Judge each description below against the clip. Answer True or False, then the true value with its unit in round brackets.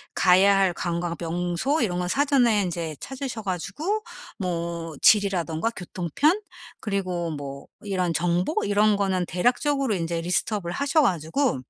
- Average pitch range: True (4.5 semitones)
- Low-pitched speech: False (185 Hz)